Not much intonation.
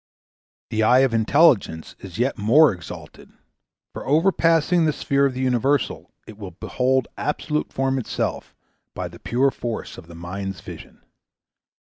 No: average, 5.2 semitones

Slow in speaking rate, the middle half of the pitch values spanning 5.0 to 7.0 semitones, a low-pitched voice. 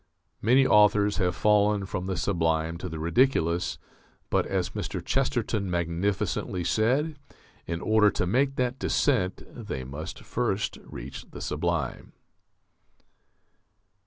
Yes: slow, 120 wpm; wide, 5.5 semitones; low, 100 Hz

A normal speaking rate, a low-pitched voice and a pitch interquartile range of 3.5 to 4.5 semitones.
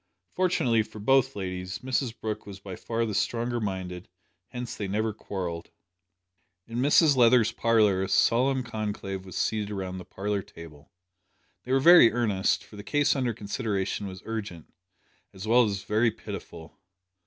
Yes: average, 155 wpm; low, 105 Hz; average, 3.8 semitones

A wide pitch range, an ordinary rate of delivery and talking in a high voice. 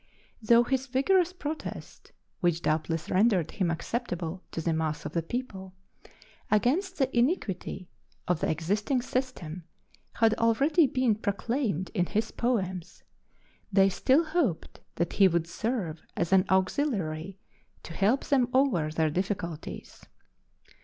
No: wide, 6.9 semitones; slow, 130 wpm; high, 200 Hz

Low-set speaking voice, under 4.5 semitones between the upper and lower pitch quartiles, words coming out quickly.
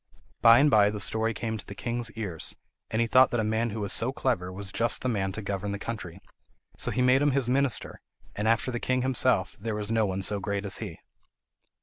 Yes: low, 110 Hz; average, 3.1 semitones; fast, 240 wpm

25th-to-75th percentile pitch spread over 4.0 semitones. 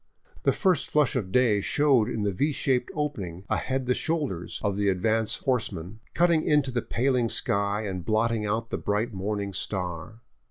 Yes: average, 4.6 semitones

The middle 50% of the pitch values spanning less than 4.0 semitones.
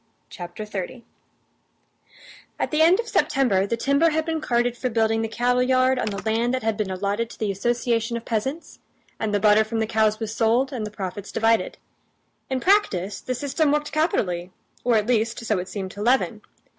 Yes: average, 3.5 semitones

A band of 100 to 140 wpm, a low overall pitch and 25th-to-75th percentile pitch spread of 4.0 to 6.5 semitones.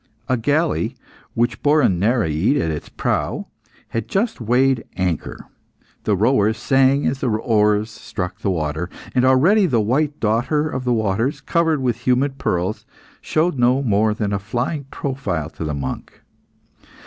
No: average, 155 wpm; low, 120 Hz; average, 4.8 semitones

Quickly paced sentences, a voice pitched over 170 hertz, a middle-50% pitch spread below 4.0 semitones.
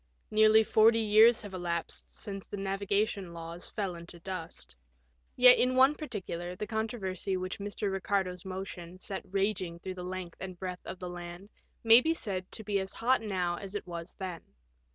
No: average, 175 wpm; high, 190 Hz; average, 3.0 semitones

